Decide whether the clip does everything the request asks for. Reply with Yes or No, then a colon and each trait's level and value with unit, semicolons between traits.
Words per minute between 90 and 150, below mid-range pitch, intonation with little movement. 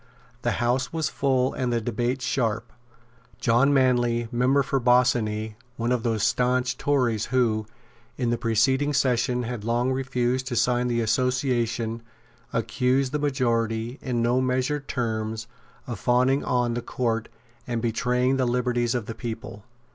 Yes: average, 145 wpm; low, 125 Hz; narrow, 1.7 semitones